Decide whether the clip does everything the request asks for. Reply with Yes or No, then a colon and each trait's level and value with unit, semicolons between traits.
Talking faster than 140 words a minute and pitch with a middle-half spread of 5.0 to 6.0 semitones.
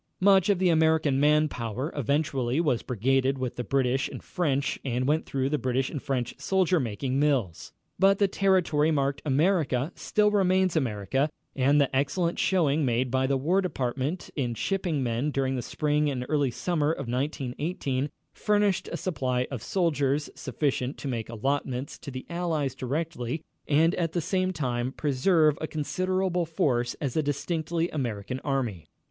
No: average, 165 wpm; average, 4.2 semitones